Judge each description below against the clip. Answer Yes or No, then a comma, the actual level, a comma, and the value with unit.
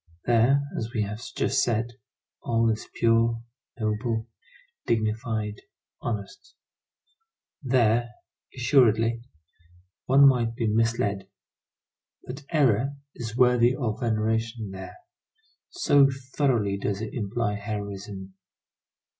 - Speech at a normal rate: No, slow, 95 wpm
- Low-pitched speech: Yes, low, 115 Hz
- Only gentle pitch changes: Yes, narrow, 2.3 semitones